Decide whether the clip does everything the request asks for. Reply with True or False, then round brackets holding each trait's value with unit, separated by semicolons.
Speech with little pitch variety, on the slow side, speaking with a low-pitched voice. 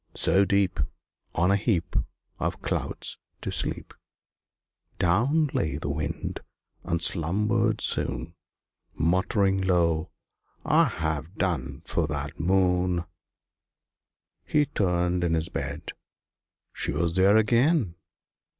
False (3.5 semitones; 105 wpm; 90 Hz)